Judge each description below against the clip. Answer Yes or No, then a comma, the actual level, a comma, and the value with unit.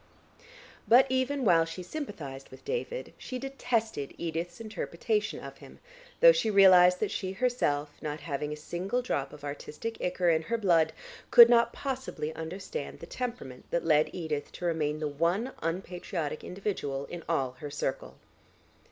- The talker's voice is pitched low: No, medium, 175 Hz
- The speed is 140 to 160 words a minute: Yes, average, 155 wpm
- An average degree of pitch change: No, wide, 7.3 semitones